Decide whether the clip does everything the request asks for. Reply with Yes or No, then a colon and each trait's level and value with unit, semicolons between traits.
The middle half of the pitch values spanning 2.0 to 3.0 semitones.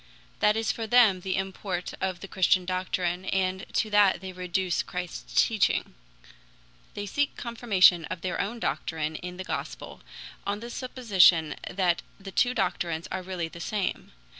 Yes: narrow, 2.4 semitones